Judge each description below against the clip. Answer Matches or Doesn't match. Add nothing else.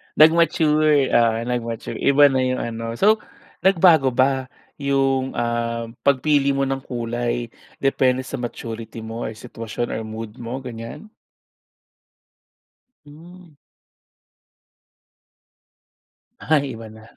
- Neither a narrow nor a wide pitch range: Matches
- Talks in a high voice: Doesn't match